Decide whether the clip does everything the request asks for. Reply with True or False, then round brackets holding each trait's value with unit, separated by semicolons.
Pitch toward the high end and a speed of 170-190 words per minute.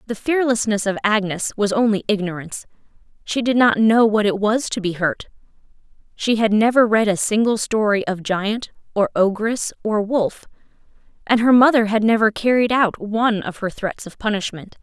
True (215 Hz; 175 wpm)